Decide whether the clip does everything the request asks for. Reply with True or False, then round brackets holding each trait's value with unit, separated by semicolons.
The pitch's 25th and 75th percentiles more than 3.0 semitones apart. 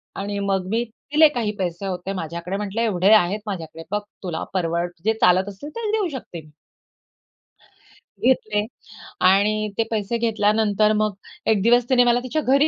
True (3.8 semitones)